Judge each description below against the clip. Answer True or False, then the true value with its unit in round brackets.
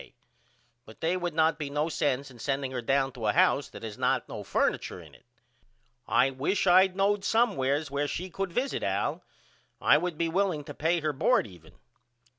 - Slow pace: False (200 wpm)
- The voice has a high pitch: False (150 Hz)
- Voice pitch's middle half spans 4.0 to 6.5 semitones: True (5.1 semitones)